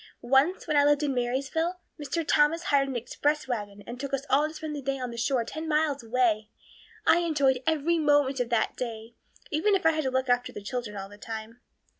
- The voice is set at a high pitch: Yes, very high, 270 Hz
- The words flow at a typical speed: No, fast, 225 wpm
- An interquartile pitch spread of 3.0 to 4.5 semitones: Yes, average, 3.9 semitones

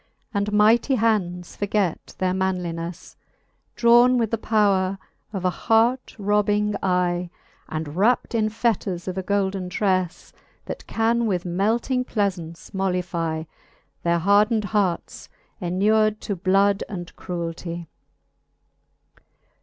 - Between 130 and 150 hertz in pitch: No, high, 195 Hz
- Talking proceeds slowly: Yes, slow, 115 wpm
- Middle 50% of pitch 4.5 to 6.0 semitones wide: No, average, 3.3 semitones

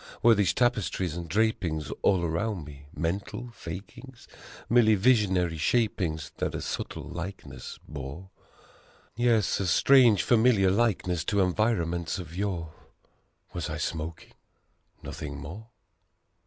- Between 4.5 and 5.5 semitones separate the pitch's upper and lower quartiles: Yes, average, 5.1 semitones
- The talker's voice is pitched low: Yes, very low, 95 Hz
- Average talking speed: No, slow, 115 wpm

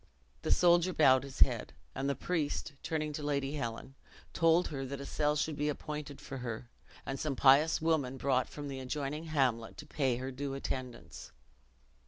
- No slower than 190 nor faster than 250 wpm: No, average, 180 wpm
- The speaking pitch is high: No, medium, 140 Hz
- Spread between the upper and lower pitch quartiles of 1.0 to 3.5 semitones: Yes, narrow, 2.4 semitones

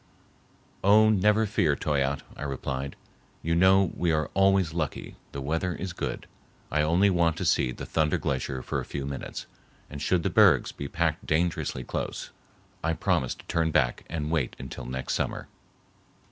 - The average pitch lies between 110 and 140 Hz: No, very low, 80 Hz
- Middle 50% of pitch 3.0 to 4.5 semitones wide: Yes, average, 4.2 semitones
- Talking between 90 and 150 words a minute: No, average, 165 wpm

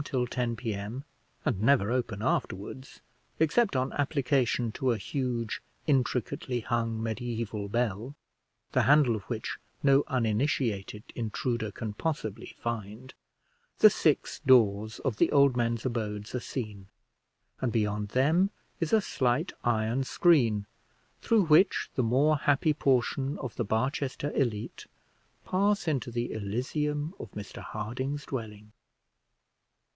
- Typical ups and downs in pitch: Yes, average, 4.2 semitones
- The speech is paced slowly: Yes, slow, 125 wpm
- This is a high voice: No, low, 120 Hz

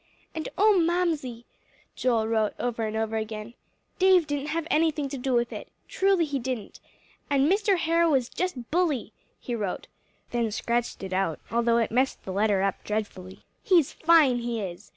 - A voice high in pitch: Yes, high, 245 Hz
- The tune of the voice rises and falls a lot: Yes, wide, 6.7 semitones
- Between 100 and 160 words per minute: No, average, 170 wpm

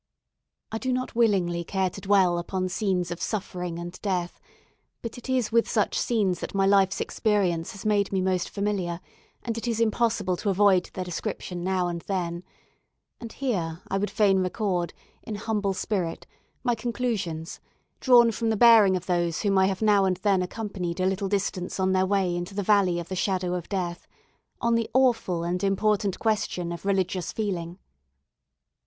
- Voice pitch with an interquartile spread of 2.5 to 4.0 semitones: Yes, average, 3.0 semitones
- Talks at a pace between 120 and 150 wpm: No, average, 180 wpm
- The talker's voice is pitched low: No, high, 195 Hz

